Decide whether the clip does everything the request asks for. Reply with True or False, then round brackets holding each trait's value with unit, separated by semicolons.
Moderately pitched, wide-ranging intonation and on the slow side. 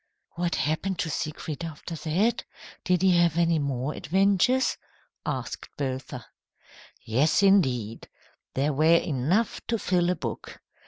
False (165 Hz; 4.5 semitones; 125 wpm)